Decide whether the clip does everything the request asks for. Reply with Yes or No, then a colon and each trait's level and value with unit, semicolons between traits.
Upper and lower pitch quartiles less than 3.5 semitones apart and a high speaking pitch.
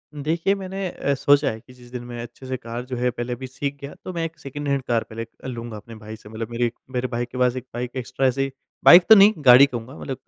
No: average, 2.9 semitones; low, 125 Hz